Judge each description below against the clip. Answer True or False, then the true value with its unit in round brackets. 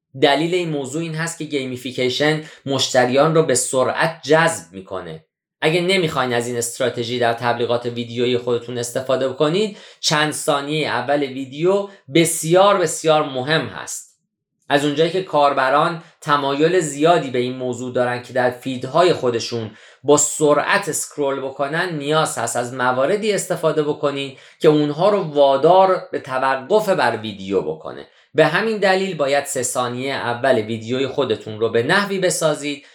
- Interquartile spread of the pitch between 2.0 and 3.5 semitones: False (4.4 semitones)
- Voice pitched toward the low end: False (145 Hz)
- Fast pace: False (140 wpm)